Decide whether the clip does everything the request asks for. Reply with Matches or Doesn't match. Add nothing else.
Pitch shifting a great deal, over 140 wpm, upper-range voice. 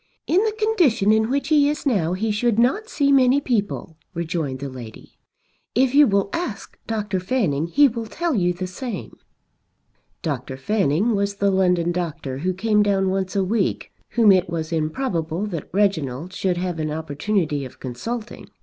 Matches